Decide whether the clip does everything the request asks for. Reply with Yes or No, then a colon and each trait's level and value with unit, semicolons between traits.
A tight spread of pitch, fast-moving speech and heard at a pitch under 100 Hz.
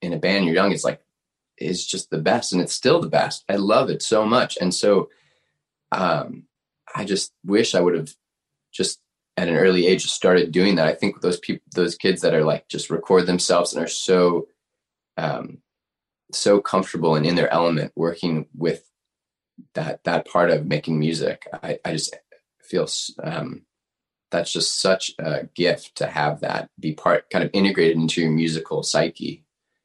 No: narrow, 2.1 semitones; average, 180 wpm; very low, 85 Hz